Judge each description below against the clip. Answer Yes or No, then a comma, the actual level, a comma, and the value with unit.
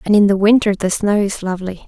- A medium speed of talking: No, fast, 255 wpm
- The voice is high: Yes, high, 200 Hz